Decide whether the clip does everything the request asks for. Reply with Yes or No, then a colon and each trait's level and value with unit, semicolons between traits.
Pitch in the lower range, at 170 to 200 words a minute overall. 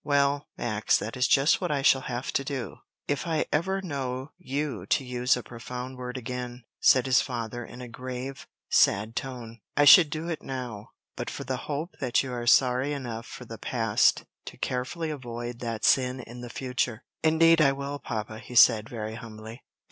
Yes: low, 125 Hz; average, 190 wpm